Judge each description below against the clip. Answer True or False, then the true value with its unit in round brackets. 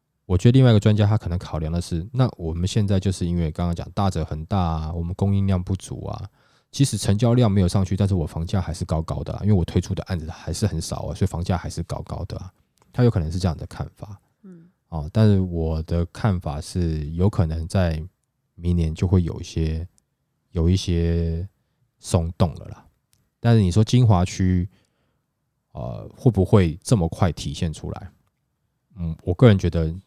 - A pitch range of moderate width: True (4.0 semitones)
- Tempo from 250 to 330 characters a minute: True (290 characters per minute)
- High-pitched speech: False (95 Hz)